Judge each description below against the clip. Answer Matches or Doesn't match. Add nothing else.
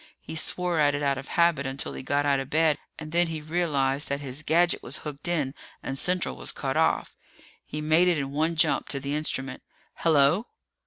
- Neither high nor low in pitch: Matches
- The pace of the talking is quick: Matches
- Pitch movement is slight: Doesn't match